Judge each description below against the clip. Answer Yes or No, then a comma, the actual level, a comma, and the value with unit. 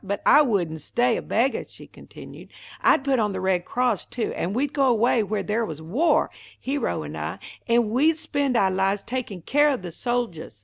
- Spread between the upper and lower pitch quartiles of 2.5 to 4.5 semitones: No, average, 5.2 semitones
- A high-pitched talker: Yes, high, 230 Hz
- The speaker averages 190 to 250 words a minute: Yes, fast, 205 wpm